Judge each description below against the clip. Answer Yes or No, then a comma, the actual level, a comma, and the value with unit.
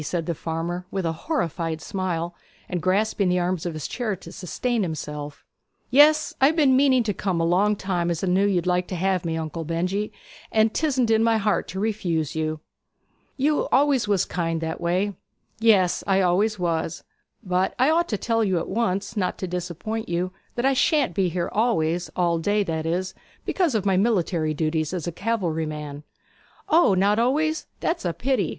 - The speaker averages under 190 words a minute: No, average, 195 wpm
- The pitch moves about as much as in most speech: Yes, average, 4.7 semitones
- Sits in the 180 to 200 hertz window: Yes, medium, 185 Hz